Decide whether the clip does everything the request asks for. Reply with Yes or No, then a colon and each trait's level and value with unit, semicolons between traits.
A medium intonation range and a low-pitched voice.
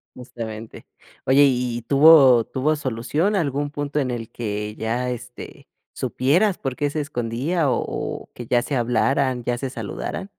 Yes: average, 3.3 semitones; low, 130 Hz